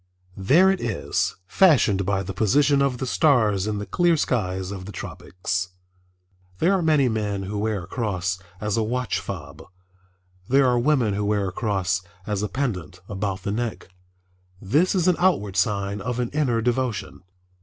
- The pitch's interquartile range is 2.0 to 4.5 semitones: No, average, 5.2 semitones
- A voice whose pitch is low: Yes, low, 105 Hz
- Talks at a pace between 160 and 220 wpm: Yes, average, 175 wpm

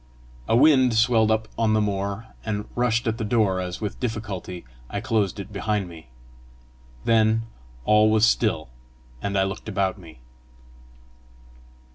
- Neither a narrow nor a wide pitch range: No, narrow, 2.3 semitones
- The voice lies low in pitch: Yes, low, 110 Hz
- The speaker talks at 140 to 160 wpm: Yes, average, 145 wpm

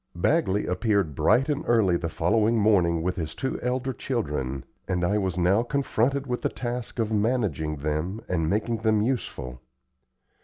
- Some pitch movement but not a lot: No, wide, 5.7 semitones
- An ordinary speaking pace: Yes, average, 160 wpm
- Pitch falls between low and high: No, low, 105 Hz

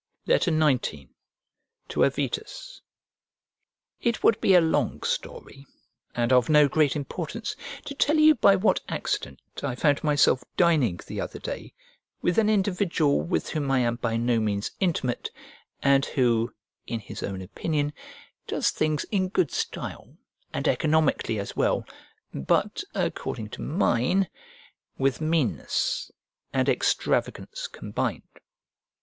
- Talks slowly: Yes, slow, 130 wpm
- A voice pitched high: No, medium, 150 Hz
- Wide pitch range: Yes, wide, 7.2 semitones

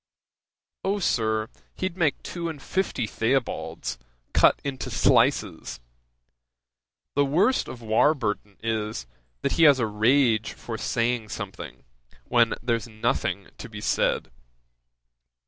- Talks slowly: Yes, slow, 115 wpm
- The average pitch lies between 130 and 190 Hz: No, low, 120 Hz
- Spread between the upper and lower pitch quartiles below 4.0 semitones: No, average, 4.6 semitones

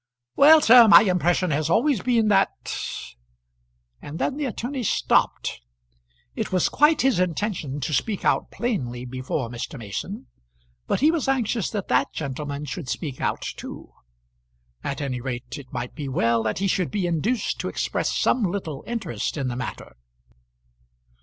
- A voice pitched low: No, medium, 165 Hz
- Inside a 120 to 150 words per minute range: No, average, 160 wpm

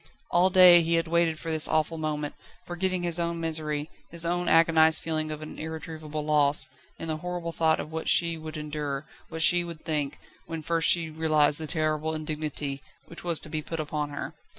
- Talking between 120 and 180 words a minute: No, average, 195 wpm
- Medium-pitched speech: Yes, medium, 160 Hz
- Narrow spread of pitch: Yes, narrow, 1.6 semitones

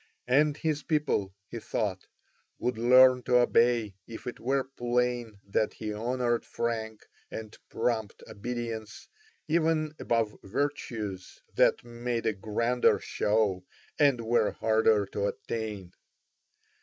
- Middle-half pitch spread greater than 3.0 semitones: No, narrow, 2.5 semitones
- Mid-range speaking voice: No, low, 115 Hz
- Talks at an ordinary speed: No, slow, 120 wpm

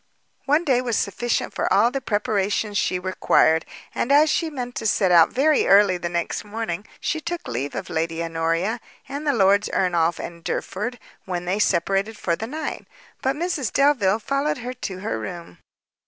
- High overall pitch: Yes, high, 210 Hz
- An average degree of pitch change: No, wide, 6.5 semitones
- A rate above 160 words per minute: Yes, average, 180 wpm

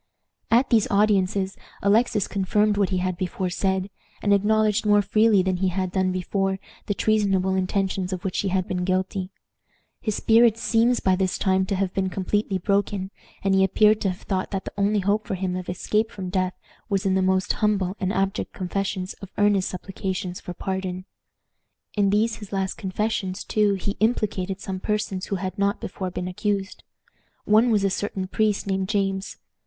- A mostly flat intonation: Yes, narrow, 1.7 semitones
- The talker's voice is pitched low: No, high, 195 Hz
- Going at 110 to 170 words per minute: No, average, 185 wpm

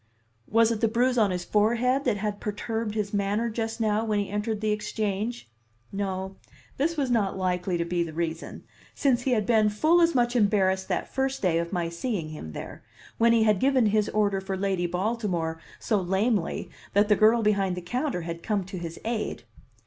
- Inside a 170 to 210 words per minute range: Yes, average, 200 wpm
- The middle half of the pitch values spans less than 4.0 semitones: Yes, average, 3.5 semitones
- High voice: Yes, high, 210 Hz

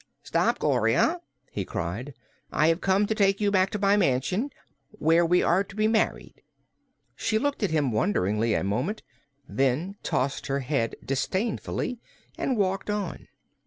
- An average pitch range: No, wide, 7.5 semitones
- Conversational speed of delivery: Yes, average, 155 wpm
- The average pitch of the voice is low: No, medium, 180 Hz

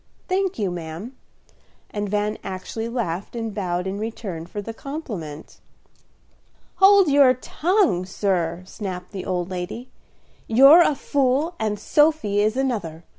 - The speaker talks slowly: Yes, slow, 130 wpm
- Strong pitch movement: Yes, wide, 6.7 semitones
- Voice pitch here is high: Yes, high, 210 Hz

